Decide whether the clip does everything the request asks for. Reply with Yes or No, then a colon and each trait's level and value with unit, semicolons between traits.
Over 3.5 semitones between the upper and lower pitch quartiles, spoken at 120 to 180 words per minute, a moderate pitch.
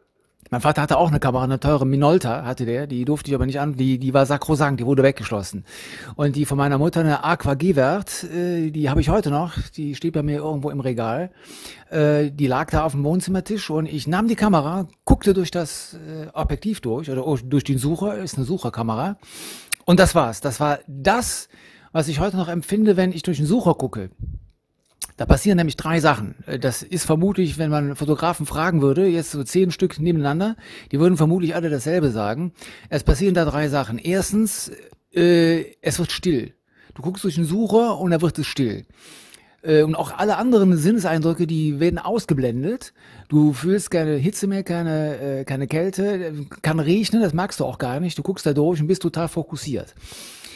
No: average, 4.0 semitones; fast, 190 wpm; medium, 155 Hz